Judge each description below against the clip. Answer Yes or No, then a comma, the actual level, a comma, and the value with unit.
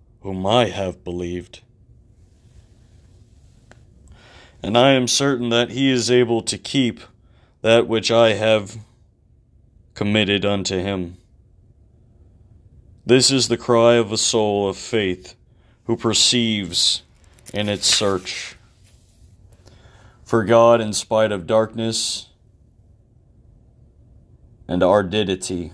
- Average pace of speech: No, slow, 100 wpm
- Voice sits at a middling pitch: No, low, 105 Hz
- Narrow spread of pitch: No, average, 3.2 semitones